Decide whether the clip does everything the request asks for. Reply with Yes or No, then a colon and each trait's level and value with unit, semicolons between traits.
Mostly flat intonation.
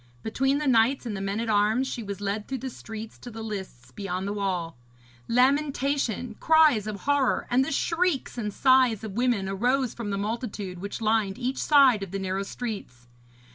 No: average, 4.6 semitones